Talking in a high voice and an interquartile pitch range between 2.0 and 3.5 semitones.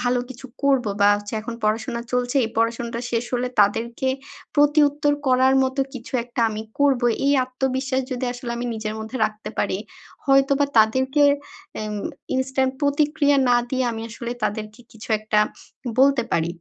Yes: very high, 250 Hz; average, 3.2 semitones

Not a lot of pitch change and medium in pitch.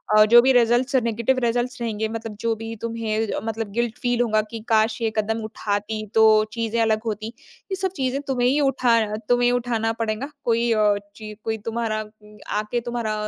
No: narrow, 1.9 semitones; high, 225 Hz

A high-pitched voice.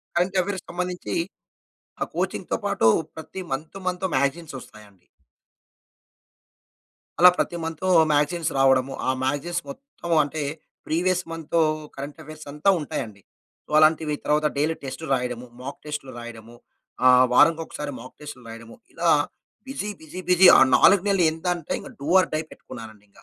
No: medium, 150 Hz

